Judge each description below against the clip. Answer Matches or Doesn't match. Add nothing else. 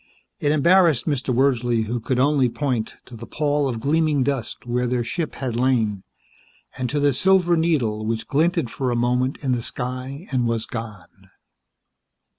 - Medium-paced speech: Matches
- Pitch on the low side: Matches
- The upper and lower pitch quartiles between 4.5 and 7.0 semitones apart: Doesn't match